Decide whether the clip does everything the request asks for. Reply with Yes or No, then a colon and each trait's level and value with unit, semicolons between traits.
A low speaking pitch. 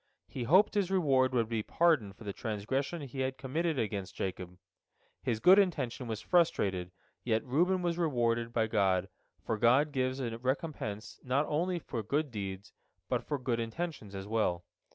Yes: low, 125 Hz